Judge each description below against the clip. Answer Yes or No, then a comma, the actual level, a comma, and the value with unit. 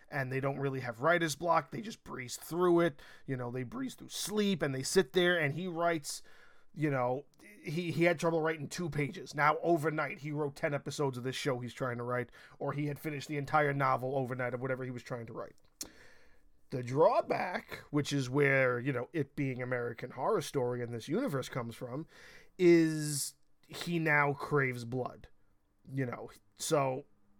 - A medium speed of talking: Yes, average, 190 wpm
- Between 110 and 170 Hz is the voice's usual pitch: Yes, medium, 140 Hz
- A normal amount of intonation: Yes, average, 4.0 semitones